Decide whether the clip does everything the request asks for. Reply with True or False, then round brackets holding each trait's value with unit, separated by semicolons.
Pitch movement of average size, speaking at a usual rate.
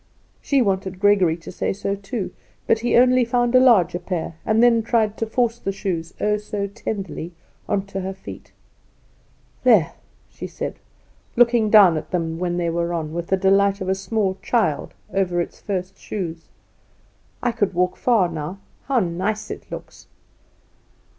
True (3.9 semitones; 170 wpm)